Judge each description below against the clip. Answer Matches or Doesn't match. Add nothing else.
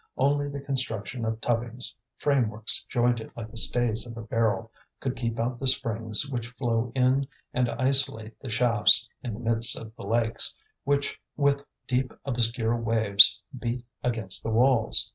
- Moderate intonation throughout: Doesn't match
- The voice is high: Doesn't match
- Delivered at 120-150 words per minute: Doesn't match